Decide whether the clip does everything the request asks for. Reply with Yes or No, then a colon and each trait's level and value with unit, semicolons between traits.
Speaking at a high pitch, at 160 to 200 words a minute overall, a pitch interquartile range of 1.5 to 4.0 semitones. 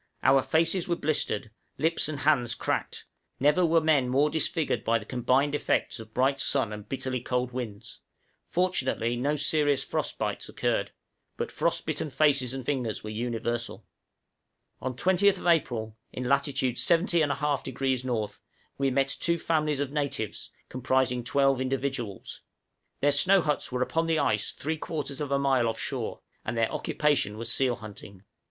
No: low, 135 Hz; average, 165 wpm; average, 3.6 semitones